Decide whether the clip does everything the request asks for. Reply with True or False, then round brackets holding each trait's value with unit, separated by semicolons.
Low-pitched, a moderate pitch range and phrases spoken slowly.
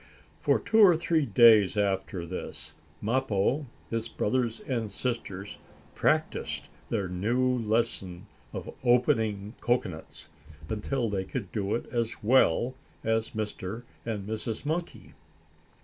True (115 Hz; 3.8 semitones; 115 wpm)